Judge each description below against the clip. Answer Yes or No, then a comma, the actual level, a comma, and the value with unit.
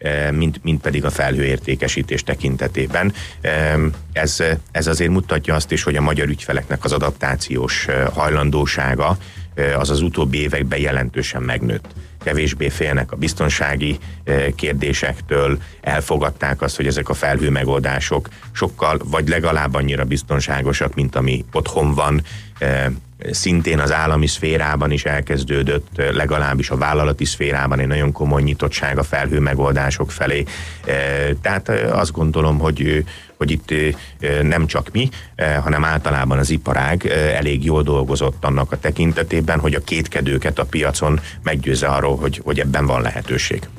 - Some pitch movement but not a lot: No, narrow, 1.9 semitones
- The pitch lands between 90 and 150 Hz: No, very low, 75 Hz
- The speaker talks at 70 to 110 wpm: No, average, 130 wpm